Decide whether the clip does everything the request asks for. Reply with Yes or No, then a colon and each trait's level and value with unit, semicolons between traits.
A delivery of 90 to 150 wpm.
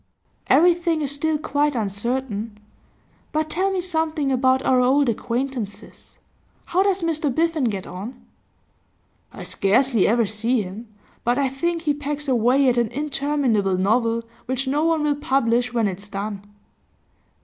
Yes: average, 145 wpm